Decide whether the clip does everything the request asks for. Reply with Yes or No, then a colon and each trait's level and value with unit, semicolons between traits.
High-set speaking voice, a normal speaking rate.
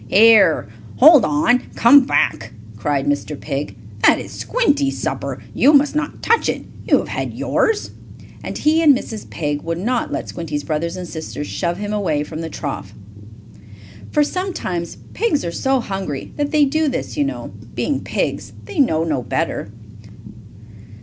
Yes: high, 200 Hz; average, 165 wpm